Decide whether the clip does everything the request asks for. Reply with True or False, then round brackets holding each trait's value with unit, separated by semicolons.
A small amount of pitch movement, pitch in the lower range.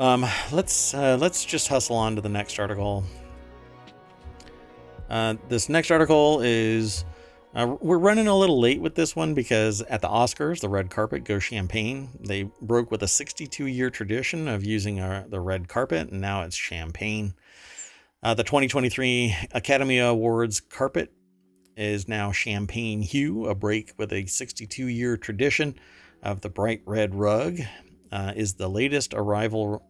False (4.3 semitones; 110 Hz)